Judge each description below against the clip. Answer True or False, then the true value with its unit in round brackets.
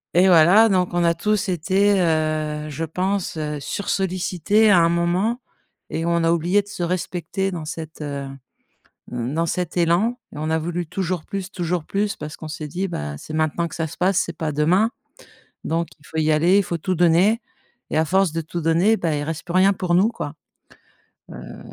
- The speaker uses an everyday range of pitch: True (3.1 semitones)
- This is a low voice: False (170 Hz)